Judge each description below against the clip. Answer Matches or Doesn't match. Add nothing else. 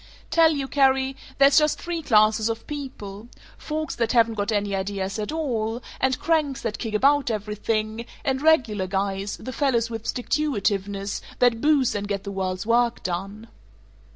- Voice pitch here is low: Doesn't match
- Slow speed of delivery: Doesn't match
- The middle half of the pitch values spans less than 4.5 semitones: Doesn't match